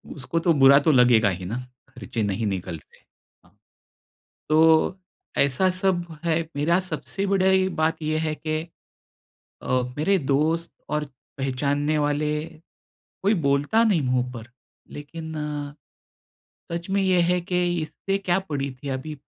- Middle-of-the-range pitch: Yes, medium, 155 Hz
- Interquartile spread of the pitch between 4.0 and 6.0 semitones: Yes, average, 4.7 semitones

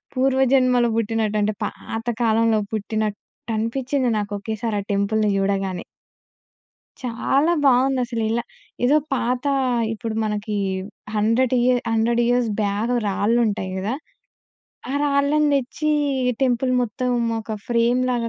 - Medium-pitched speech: No, high, 230 Hz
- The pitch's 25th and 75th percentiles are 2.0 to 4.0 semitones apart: Yes, average, 2.8 semitones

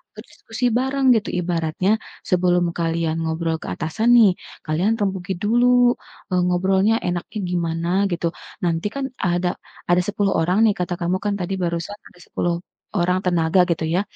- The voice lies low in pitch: No, medium, 180 Hz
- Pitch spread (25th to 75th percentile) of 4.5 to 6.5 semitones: No, average, 3.1 semitones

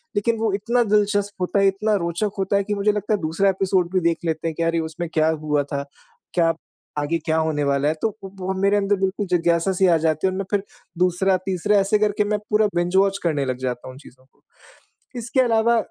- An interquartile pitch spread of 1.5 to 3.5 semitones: No, average, 4.0 semitones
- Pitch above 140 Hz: Yes, high, 190 Hz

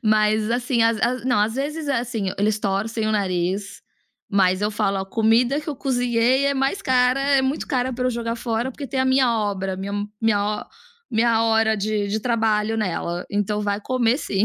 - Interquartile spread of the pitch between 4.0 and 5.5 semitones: No, average, 3.4 semitones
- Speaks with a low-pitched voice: No, high, 225 Hz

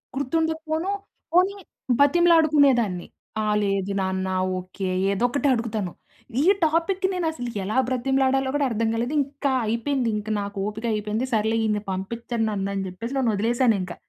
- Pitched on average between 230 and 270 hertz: Yes, high, 235 Hz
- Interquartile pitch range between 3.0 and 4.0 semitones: No, wide, 5.6 semitones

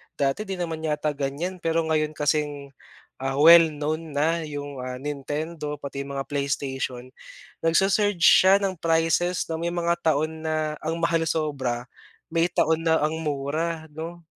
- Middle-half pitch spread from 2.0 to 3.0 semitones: Yes, narrow, 2.5 semitones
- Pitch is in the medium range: Yes, medium, 155 Hz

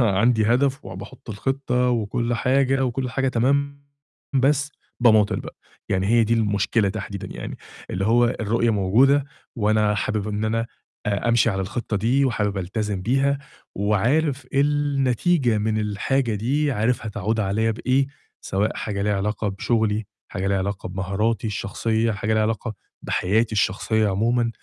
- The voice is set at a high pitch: No, low, 110 Hz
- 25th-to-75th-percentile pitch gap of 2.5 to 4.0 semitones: Yes, average, 3.5 semitones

